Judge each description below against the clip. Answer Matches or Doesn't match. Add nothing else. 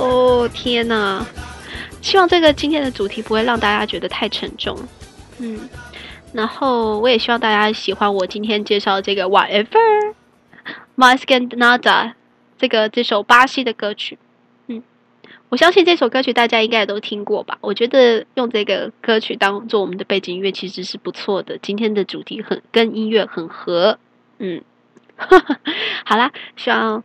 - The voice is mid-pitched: Doesn't match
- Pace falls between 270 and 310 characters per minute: Matches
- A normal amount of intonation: Matches